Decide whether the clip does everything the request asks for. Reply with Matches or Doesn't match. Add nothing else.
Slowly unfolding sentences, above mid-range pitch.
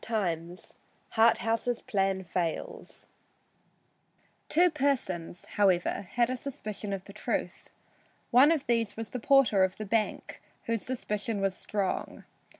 Matches